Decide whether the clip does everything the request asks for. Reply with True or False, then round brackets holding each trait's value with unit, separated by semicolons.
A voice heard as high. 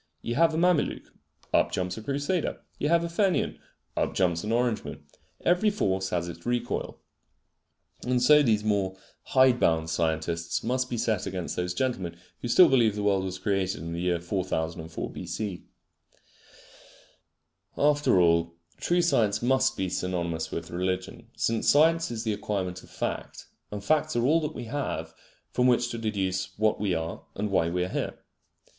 False (105 Hz)